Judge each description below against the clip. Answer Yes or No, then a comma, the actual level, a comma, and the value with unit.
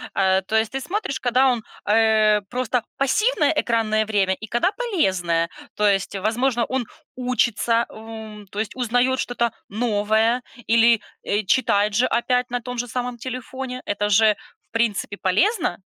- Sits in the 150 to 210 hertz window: No, high, 230 Hz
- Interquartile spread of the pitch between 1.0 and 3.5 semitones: Yes, average, 3.1 semitones